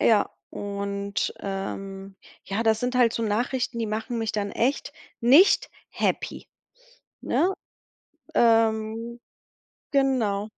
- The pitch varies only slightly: No, average, 3.0 semitones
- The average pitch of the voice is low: No, high, 225 Hz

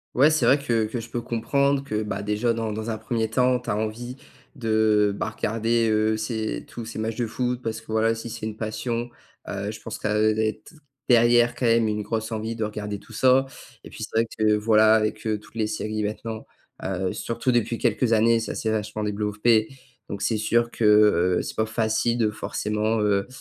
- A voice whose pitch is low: Yes, low, 110 Hz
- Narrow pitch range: Yes, narrow, 1.5 semitones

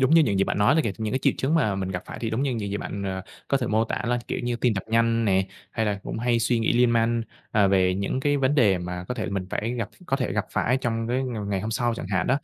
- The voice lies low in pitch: Yes, low, 115 Hz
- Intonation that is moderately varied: Yes, average, 3.7 semitones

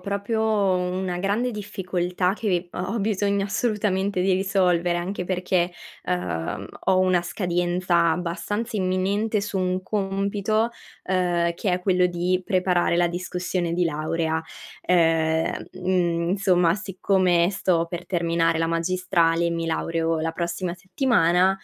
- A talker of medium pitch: Yes, medium, 180 Hz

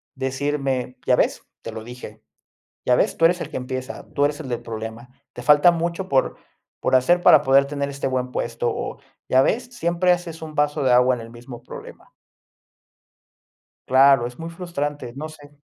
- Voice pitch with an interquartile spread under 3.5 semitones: No, average, 3.8 semitones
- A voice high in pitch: No, low, 135 Hz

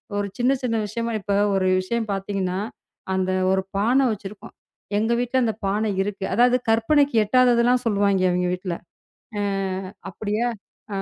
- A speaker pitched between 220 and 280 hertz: No, high, 210 Hz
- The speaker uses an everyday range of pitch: Yes, average, 3.5 semitones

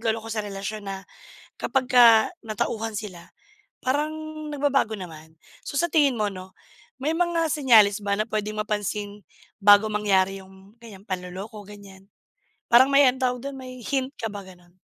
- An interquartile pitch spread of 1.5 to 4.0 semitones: No, average, 4.6 semitones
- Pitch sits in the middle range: No, high, 215 Hz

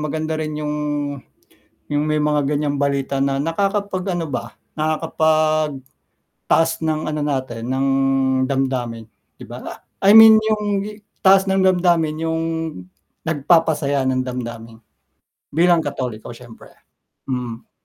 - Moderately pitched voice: Yes, medium, 150 Hz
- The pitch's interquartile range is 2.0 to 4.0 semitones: Yes, average, 3.6 semitones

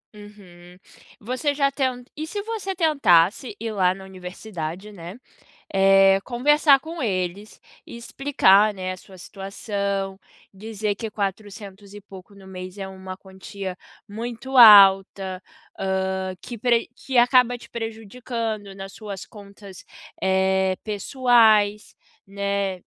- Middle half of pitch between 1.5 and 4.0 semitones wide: Yes, average, 3.6 semitones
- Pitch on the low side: No, high, 200 Hz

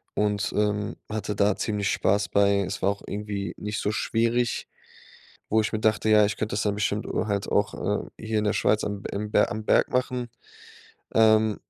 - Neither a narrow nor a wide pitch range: No, narrow, 1.2 semitones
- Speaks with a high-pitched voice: No, low, 105 Hz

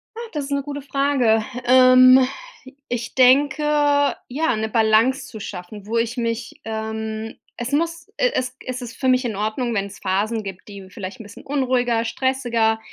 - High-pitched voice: Yes, high, 240 Hz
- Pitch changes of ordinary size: Yes, average, 3.4 semitones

